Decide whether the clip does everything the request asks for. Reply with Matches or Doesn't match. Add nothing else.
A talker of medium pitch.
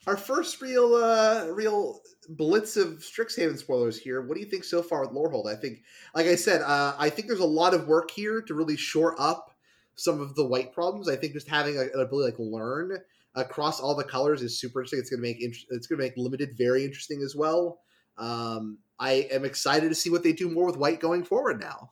Matches